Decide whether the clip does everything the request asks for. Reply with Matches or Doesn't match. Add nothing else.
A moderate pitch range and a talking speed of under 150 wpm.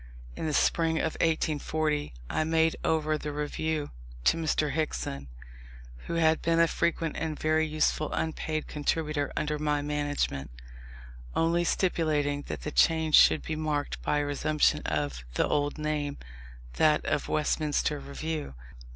Doesn't match